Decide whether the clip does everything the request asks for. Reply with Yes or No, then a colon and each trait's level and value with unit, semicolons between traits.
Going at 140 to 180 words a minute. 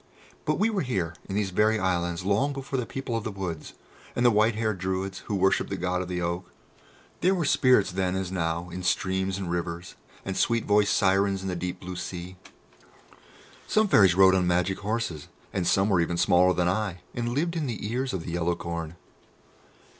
No: fast, 205 wpm